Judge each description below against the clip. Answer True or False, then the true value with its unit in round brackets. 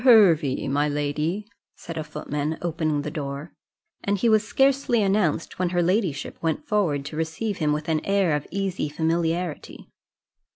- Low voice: False (165 Hz)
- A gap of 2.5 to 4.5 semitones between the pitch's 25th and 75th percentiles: False (4.9 semitones)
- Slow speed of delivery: False (160 wpm)